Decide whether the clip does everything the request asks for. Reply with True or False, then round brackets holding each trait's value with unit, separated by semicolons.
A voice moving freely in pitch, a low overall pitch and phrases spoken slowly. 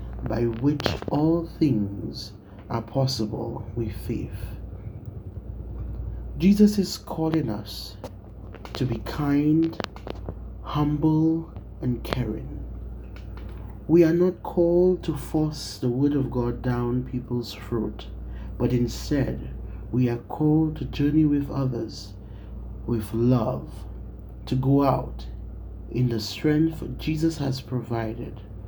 True (6.1 semitones; 120 Hz; 105 wpm)